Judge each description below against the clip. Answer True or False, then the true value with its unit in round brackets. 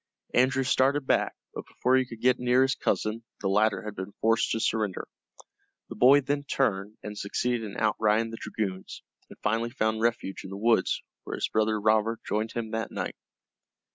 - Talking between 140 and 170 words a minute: False (185 wpm)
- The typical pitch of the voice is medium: False (110 Hz)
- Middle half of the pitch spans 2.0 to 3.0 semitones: True (2.6 semitones)